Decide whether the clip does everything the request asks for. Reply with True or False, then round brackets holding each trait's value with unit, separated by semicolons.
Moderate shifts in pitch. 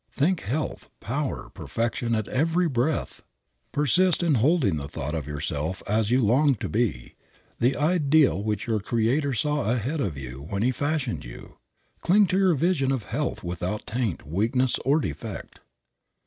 False (6.6 semitones)